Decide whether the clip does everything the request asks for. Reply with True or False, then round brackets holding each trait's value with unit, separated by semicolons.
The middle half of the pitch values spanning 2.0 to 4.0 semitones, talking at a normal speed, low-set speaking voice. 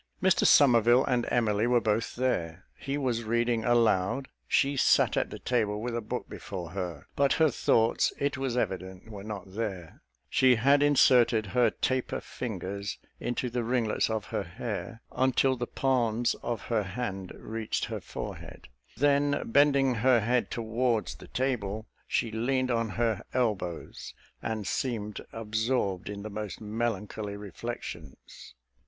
True (3.3 semitones; 150 wpm; 115 Hz)